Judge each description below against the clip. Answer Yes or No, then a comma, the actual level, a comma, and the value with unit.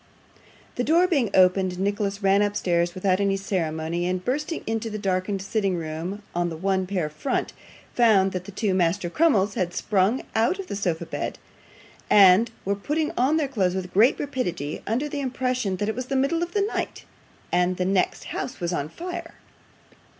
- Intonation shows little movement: No, average, 5.3 semitones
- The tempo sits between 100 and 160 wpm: No, average, 185 wpm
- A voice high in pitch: Yes, high, 200 Hz